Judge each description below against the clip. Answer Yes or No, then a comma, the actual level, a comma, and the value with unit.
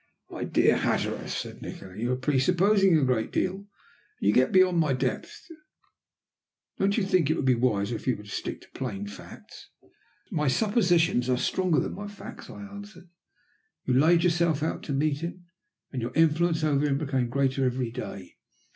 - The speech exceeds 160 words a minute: Yes, average, 180 wpm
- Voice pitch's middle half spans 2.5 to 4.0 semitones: No, wide, 5.6 semitones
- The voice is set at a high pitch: No, medium, 150 Hz